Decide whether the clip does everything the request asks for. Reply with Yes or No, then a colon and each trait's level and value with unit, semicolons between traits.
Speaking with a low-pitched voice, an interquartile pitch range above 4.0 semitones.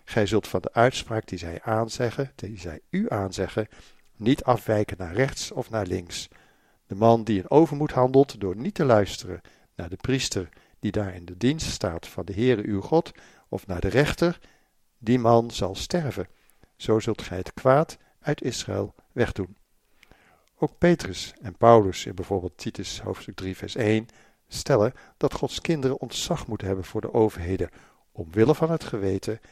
Yes: low, 110 Hz; average, 5.0 semitones